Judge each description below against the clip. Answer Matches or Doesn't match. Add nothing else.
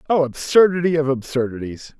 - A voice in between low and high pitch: Matches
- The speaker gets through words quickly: Doesn't match